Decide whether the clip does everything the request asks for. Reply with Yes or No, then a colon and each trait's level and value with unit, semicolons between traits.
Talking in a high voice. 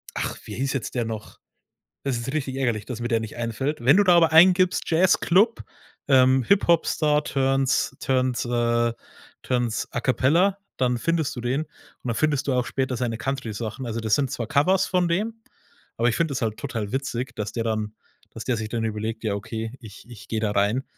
No: low, 125 Hz